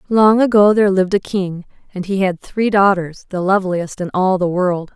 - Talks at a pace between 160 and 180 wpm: No, fast, 205 wpm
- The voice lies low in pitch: No, high, 190 Hz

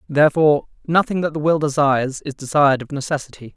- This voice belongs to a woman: No, male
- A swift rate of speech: No, average, 170 wpm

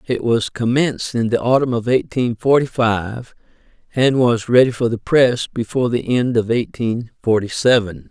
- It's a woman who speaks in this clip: No, male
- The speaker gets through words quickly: No, average, 170 wpm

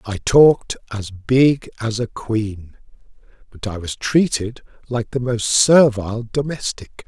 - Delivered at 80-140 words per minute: Yes, slow, 135 wpm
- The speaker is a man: Yes, male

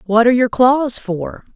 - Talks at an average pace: Yes, average, 195 wpm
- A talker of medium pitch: No, high, 235 Hz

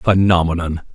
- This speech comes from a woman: No, male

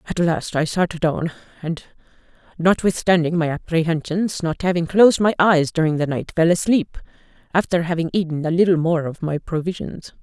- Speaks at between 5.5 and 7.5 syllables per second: No, 5.2 syllables/s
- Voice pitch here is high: No, medium, 170 Hz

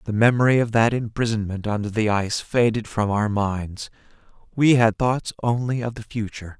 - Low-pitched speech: Yes, low, 110 Hz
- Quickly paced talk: No, average, 175 wpm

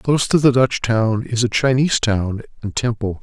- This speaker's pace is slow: No, fast, 205 wpm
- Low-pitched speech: Yes, low, 120 Hz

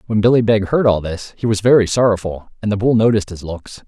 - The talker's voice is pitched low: Yes, low, 105 Hz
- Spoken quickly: Yes, fast, 250 wpm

